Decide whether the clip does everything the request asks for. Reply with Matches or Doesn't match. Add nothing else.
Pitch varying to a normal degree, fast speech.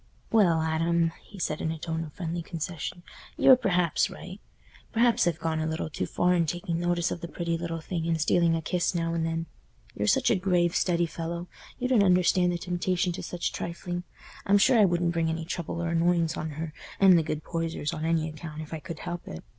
Doesn't match